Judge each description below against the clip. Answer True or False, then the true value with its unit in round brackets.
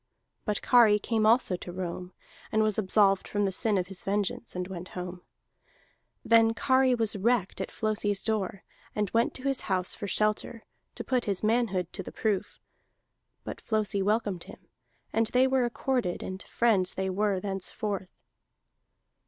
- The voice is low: False (210 Hz)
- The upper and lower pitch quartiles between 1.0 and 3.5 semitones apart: True (3.2 semitones)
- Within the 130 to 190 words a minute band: True (160 wpm)